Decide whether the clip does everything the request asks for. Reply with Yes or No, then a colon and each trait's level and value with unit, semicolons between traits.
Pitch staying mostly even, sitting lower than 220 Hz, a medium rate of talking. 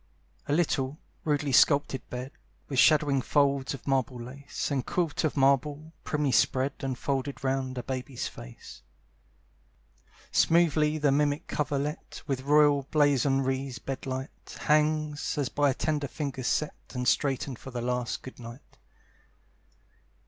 No: narrow, 2.1 semitones; medium, 140 Hz; slow, 130 wpm